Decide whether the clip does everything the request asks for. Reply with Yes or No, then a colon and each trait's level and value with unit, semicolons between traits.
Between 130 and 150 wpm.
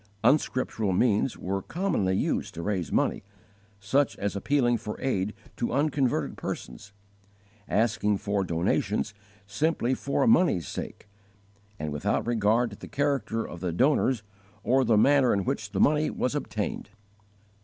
Yes: average, 140 wpm